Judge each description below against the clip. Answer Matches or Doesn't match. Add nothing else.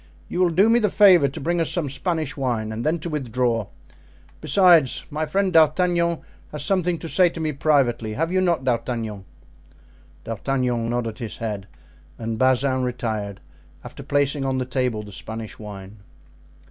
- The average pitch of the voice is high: Doesn't match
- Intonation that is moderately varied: Doesn't match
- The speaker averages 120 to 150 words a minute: Doesn't match